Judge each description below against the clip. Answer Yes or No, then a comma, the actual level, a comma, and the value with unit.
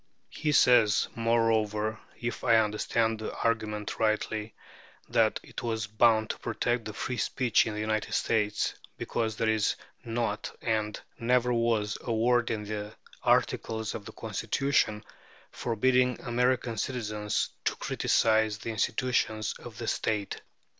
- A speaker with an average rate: No, slow, 130 wpm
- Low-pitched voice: Yes, low, 110 Hz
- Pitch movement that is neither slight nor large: No, narrow, 1.7 semitones